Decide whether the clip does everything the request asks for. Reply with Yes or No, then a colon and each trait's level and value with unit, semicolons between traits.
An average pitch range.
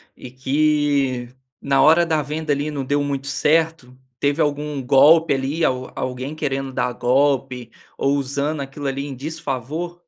No: narrow, 2.3 semitones